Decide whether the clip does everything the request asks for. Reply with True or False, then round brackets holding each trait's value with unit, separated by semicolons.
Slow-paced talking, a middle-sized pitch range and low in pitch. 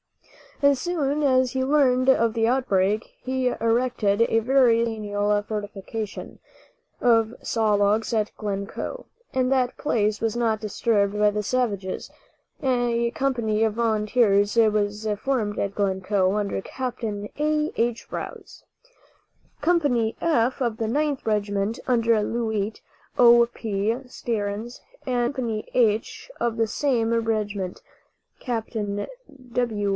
False (120 wpm; 3.1 semitones; 225 Hz)